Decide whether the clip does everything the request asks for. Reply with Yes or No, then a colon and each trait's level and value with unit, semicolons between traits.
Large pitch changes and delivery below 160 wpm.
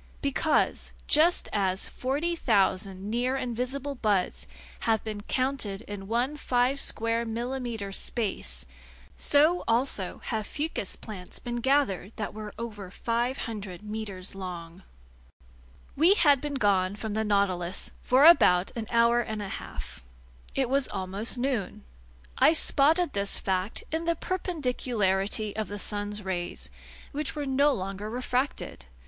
Yes: wide, 5.9 semitones; slow, 135 wpm